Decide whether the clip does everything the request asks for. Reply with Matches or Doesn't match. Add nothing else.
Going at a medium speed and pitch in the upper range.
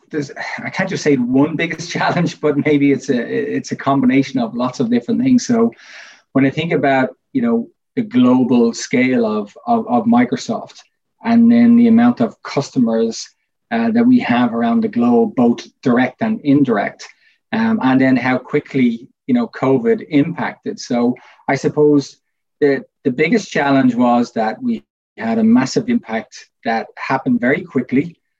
Matches